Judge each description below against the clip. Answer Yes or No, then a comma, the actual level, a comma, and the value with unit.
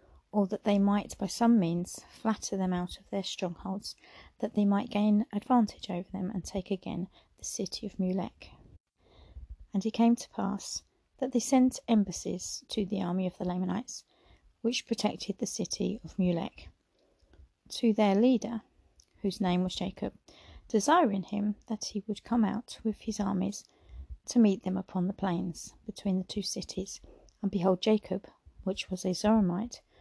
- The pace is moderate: Yes, average, 165 wpm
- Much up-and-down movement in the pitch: No, average, 2.8 semitones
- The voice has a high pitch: Yes, high, 200 Hz